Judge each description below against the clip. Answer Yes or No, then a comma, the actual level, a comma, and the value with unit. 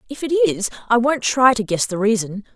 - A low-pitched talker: No, high, 225 Hz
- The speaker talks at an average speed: No, fast, 235 wpm